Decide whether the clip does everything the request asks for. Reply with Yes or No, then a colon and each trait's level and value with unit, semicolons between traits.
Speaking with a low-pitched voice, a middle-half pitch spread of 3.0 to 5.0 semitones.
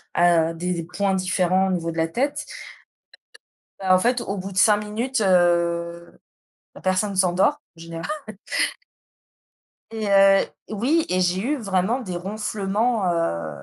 No: high, 190 Hz; average, 3.5 semitones